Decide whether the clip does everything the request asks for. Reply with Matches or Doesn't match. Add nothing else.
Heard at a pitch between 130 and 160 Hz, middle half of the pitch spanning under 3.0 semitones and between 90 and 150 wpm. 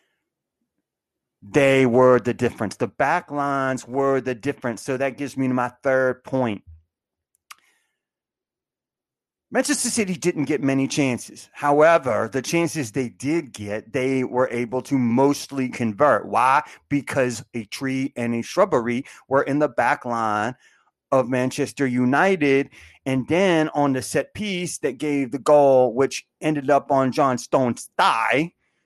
Matches